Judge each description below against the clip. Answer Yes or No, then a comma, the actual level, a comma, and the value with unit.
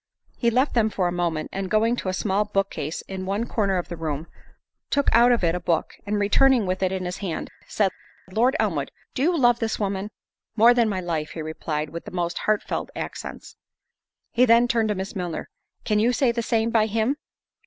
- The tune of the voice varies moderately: Yes, average, 4.5 semitones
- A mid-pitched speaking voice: No, high, 205 Hz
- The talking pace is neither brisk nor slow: No, fast, 210 wpm